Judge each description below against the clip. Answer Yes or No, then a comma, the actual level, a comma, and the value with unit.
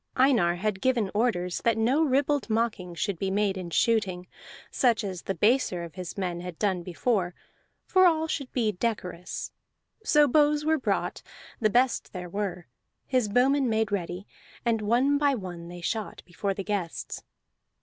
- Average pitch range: No, wide, 5.8 semitones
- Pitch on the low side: No, high, 210 Hz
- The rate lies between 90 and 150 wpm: No, average, 165 wpm